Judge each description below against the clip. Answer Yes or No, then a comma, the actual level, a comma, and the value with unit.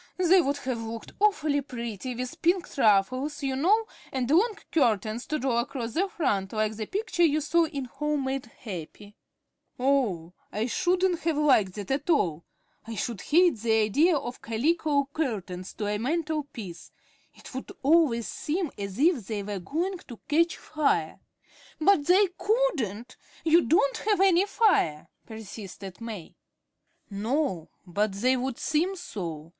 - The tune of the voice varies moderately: No, wide, 7.2 semitones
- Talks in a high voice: Yes, very high, 265 Hz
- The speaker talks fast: No, average, 155 wpm